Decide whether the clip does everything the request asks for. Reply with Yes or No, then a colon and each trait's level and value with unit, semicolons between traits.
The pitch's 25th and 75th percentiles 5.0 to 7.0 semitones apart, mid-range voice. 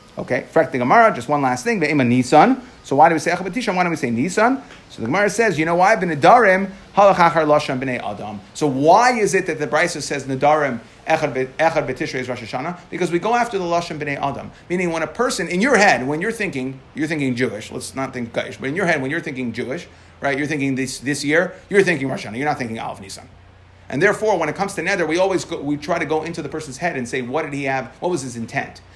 Yes: wide, 5.5 semitones; medium, 155 Hz